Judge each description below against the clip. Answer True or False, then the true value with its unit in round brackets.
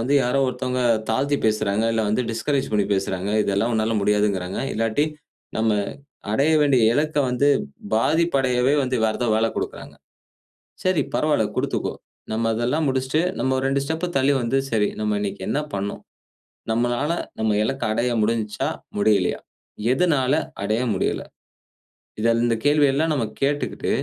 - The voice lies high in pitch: False (120 Hz)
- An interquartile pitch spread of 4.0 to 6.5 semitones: True (4.3 semitones)